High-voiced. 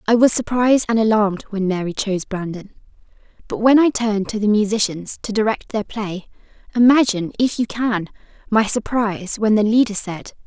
Yes: high, 215 Hz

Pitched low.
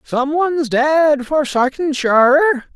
No: very high, 275 Hz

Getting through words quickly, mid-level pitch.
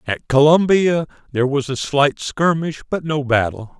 No: average, 160 wpm; medium, 145 Hz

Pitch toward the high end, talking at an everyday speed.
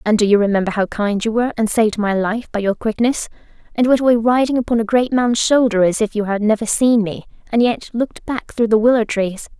No: high, 225 Hz; fast, 245 wpm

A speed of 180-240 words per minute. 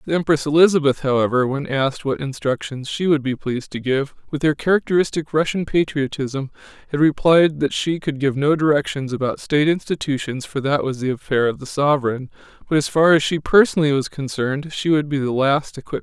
Yes: average, 200 wpm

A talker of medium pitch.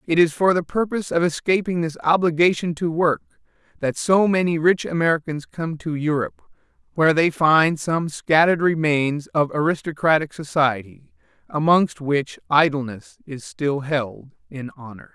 Yes: medium, 155 Hz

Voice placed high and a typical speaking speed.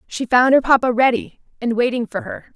No: high, 245 Hz; fast, 210 wpm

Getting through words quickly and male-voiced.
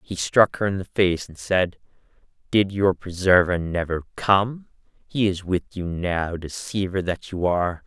No: average, 170 wpm; male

